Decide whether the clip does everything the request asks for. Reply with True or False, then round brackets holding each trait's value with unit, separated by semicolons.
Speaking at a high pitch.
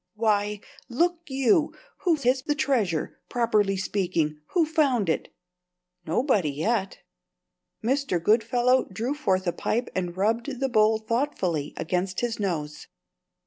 True (220 Hz)